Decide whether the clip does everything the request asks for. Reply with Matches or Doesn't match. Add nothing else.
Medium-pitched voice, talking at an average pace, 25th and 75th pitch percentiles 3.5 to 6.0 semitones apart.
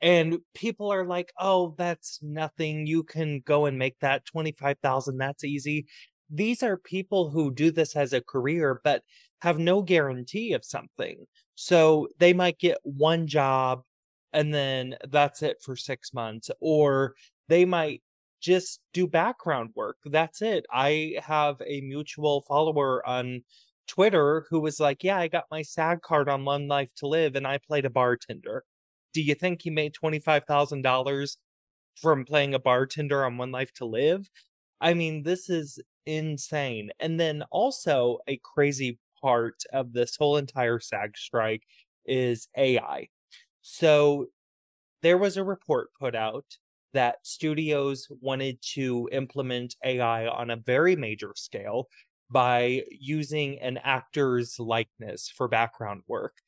Matches